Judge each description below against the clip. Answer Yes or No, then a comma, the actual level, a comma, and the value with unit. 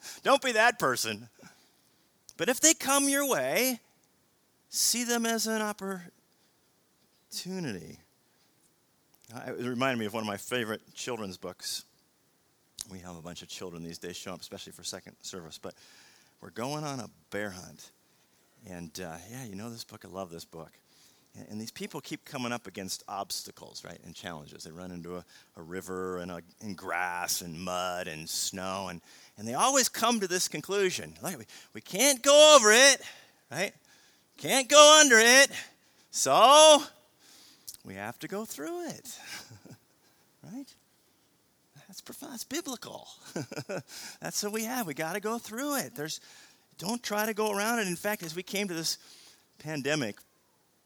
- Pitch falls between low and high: Yes, medium, 155 Hz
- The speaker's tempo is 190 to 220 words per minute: No, average, 165 wpm